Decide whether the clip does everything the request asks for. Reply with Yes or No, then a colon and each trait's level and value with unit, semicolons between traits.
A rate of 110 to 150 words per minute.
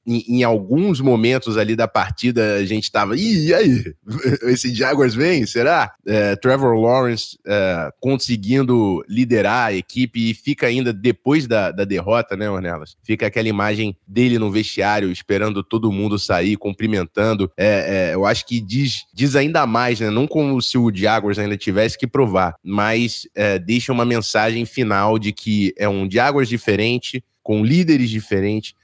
No: average, 165 wpm